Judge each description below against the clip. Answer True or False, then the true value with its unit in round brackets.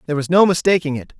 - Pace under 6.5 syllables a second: False (8.1 syllables/s)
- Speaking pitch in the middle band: True (160 Hz)